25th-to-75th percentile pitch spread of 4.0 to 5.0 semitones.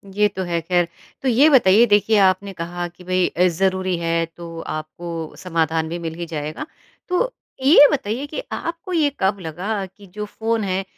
Yes: average, 4.4 semitones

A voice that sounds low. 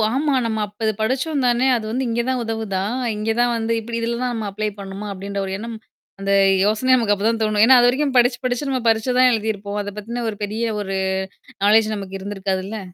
No: high, 220 Hz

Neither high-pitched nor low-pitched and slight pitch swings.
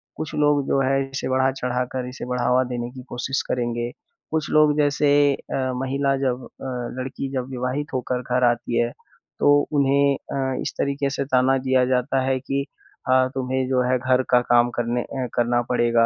No: low, 130 Hz; narrow, 1.6 semitones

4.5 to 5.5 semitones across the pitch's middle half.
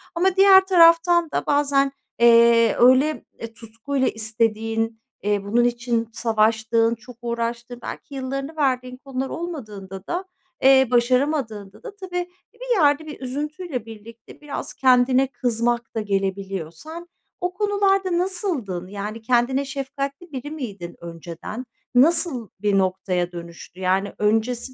Yes: average, 5.1 semitones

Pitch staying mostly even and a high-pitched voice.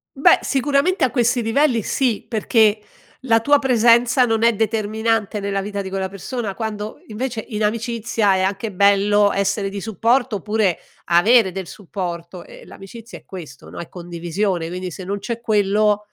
No: average, 3.0 semitones; high, 210 Hz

